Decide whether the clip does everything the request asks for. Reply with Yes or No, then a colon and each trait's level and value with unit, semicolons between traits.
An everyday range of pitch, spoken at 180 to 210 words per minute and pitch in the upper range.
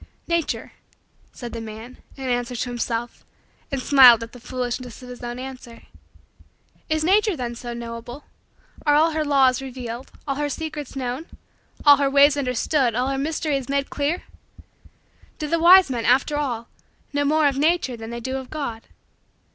No: average, 3.3 semitones; average, 170 wpm; very high, 265 Hz